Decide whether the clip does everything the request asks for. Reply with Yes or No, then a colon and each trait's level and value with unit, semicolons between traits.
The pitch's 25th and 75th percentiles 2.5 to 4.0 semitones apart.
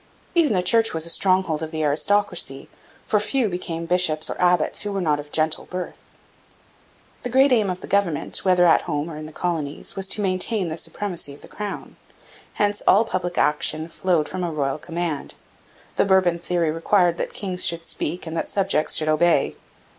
Yes: average, 3.5 semitones